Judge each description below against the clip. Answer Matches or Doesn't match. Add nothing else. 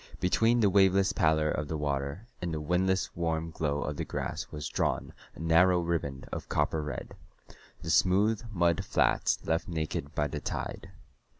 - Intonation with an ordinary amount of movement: Matches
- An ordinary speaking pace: Matches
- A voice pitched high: Doesn't match